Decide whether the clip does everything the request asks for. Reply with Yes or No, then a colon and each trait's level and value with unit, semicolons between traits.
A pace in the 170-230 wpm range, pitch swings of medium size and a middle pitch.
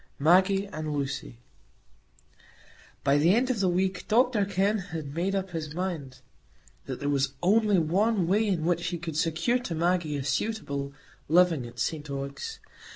No: average, 160 wpm; average, 5.0 semitones; medium, 175 Hz